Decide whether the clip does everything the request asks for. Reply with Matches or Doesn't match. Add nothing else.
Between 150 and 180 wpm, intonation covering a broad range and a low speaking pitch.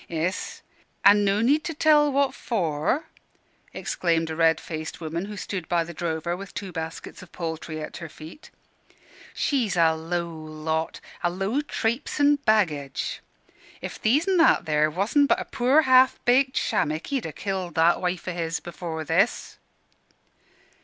Doesn't match